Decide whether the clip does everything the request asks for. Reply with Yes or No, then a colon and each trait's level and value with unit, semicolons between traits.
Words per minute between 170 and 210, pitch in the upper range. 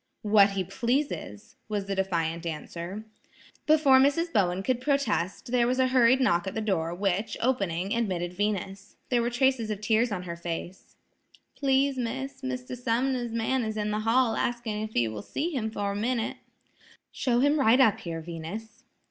Yes: average, 175 wpm; high, 220 Hz